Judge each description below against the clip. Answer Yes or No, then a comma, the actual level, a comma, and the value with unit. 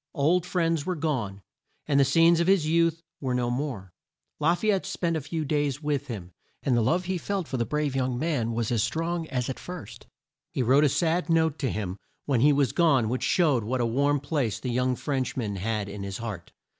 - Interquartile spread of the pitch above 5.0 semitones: Yes, wide, 5.5 semitones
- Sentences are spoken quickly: Yes, fast, 225 wpm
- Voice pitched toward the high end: No, medium, 140 Hz